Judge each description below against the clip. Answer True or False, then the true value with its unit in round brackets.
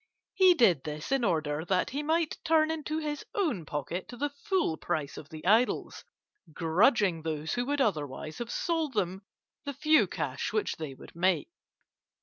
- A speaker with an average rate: True (165 wpm)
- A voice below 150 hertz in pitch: False (210 Hz)